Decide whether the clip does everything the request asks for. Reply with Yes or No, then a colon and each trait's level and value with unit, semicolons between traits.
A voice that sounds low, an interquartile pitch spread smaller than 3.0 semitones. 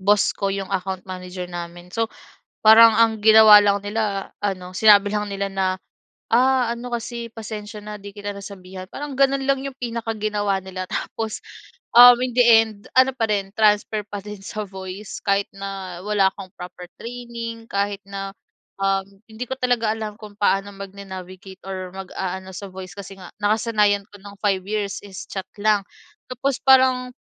No: high, 205 Hz; narrow, 2.6 semitones